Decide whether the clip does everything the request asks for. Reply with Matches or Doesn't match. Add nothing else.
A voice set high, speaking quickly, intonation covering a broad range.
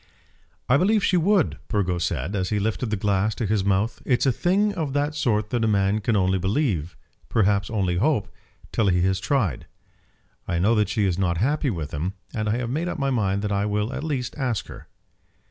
Doesn't match